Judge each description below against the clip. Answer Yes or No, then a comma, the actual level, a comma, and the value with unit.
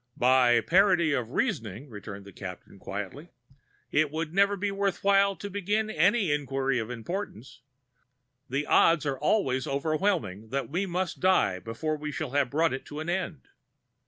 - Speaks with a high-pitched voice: No, medium, 150 Hz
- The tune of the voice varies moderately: No, wide, 7.1 semitones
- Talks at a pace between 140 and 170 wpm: Yes, average, 160 wpm